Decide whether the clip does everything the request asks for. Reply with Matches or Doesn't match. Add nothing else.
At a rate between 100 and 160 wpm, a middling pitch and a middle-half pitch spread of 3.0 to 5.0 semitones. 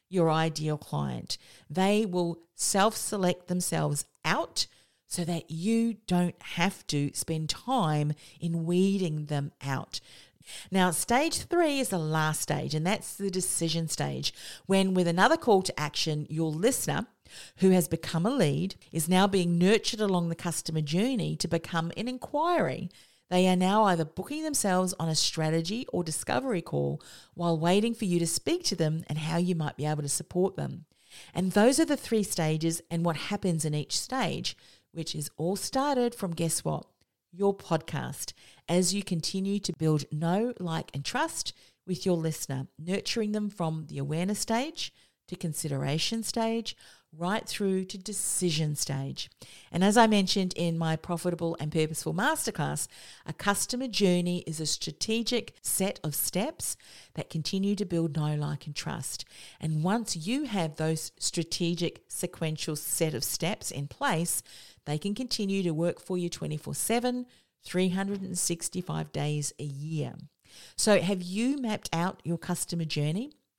Matches